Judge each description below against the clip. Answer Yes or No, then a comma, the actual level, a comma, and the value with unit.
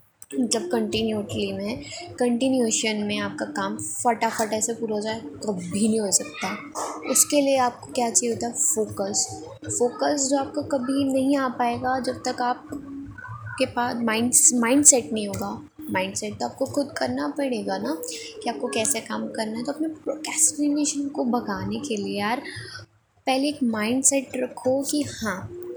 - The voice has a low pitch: No, high, 245 Hz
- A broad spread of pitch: No, average, 3.8 semitones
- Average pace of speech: Yes, average, 170 wpm